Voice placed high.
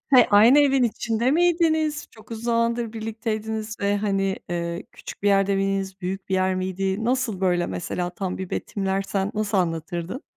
Yes: high, 205 Hz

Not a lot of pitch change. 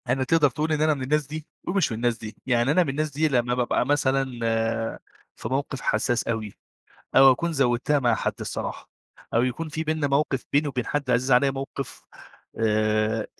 No: average, 3.6 semitones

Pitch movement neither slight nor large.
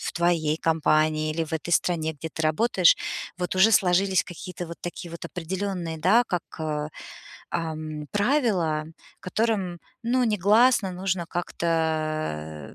Yes: average, 3.5 semitones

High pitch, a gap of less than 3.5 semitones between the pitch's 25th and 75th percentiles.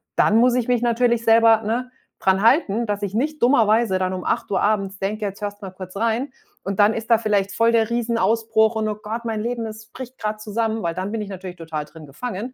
Yes: high, 220 Hz; average, 2.7 semitones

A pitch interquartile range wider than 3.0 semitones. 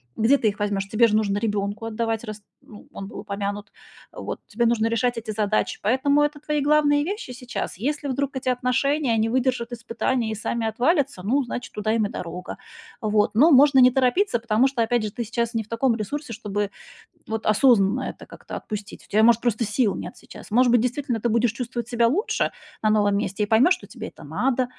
Yes: average, 3.4 semitones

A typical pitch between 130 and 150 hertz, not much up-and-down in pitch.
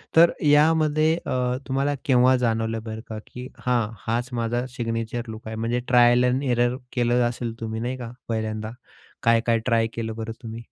No: low, 120 Hz; narrow, 1.8 semitones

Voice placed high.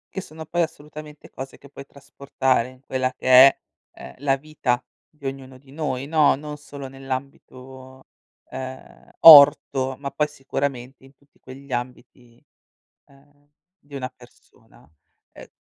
No: low, 135 Hz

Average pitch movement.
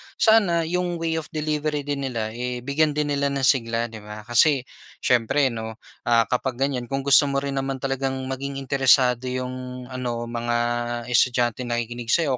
Yes: average, 3.0 semitones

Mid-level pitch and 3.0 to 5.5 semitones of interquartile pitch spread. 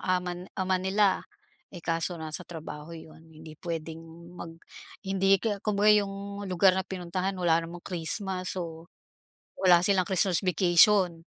No: medium, 180 Hz; narrow, 2.5 semitones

